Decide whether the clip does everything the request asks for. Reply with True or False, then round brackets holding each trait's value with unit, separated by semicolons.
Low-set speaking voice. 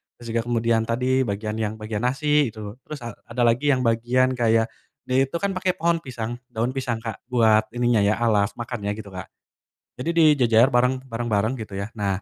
True (115 Hz)